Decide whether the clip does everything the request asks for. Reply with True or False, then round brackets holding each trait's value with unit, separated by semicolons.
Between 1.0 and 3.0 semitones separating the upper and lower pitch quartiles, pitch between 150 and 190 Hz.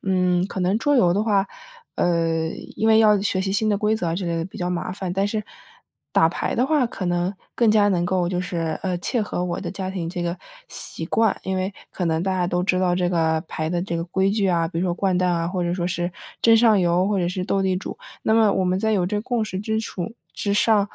True (2.7 semitones; 185 Hz)